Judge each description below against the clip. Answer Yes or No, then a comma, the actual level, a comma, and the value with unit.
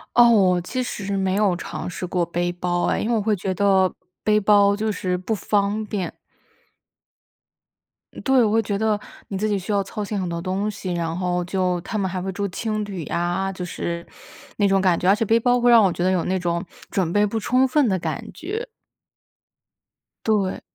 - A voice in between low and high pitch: No, high, 195 Hz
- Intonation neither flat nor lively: Yes, average, 3.0 semitones